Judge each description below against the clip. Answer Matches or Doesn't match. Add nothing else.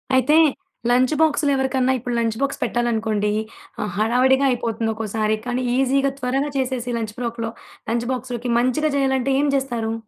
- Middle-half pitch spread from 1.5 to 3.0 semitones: Matches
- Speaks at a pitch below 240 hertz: Doesn't match